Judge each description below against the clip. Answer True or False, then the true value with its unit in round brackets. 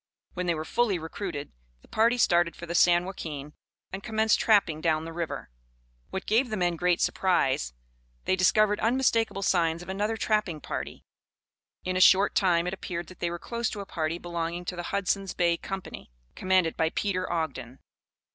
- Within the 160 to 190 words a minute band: True (180 wpm)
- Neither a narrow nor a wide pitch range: True (3.0 semitones)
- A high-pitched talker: False (180 Hz)